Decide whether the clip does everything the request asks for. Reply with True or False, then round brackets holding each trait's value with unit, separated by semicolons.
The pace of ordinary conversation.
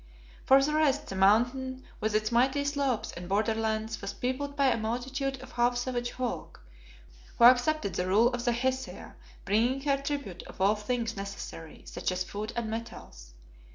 True (170 wpm)